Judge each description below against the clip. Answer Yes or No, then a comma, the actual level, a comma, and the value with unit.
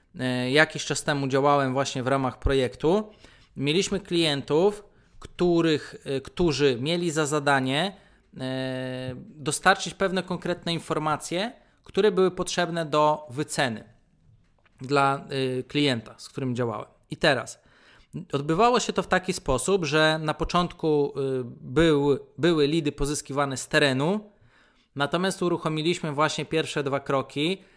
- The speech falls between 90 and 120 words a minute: Yes, slow, 110 wpm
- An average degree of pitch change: Yes, average, 4.1 semitones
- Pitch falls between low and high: Yes, medium, 150 Hz